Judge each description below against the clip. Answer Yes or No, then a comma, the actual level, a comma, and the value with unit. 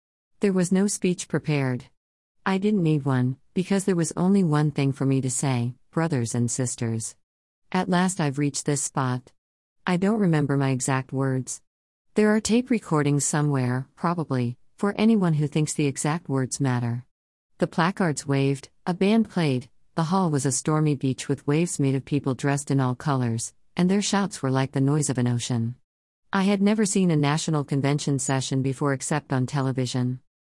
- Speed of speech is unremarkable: Yes, average, 180 wpm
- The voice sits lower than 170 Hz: Yes, medium, 140 Hz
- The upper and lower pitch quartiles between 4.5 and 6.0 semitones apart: Yes, average, 5.0 semitones